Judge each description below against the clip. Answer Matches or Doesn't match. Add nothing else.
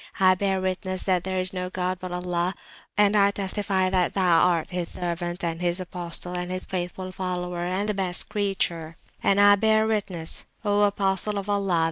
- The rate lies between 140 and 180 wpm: Doesn't match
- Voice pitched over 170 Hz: Matches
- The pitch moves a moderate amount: Doesn't match